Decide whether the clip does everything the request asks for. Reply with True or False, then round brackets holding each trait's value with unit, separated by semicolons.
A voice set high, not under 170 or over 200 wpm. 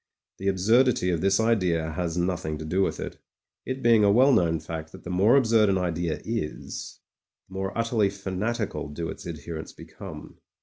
False (95 Hz; 180 wpm)